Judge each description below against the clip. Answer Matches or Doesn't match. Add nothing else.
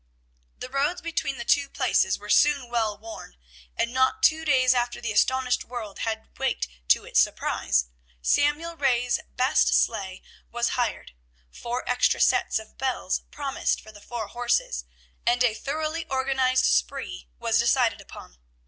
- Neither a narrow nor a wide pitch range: Matches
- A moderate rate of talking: Matches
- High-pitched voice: Matches